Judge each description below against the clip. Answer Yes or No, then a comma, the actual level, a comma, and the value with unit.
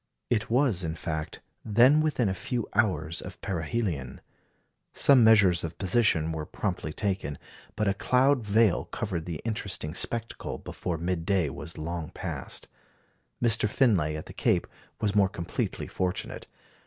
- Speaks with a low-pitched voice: Yes, very low, 95 Hz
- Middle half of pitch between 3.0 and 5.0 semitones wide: No, wide, 5.4 semitones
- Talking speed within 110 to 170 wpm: Yes, average, 145 wpm